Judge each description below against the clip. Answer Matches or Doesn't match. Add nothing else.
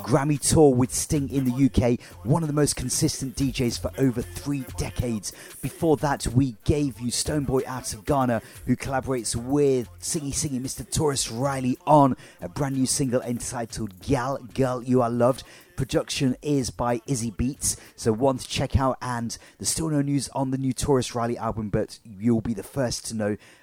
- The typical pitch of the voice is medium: Doesn't match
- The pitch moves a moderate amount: Matches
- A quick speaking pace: Doesn't match